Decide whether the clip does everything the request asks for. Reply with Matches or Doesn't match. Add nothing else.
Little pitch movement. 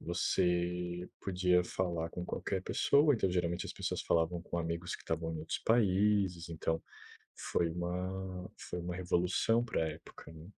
Matches